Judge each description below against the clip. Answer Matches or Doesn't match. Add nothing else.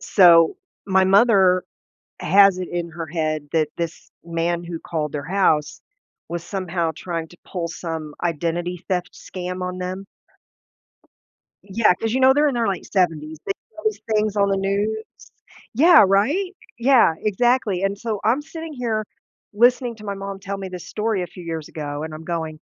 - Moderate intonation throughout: Matches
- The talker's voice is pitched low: Doesn't match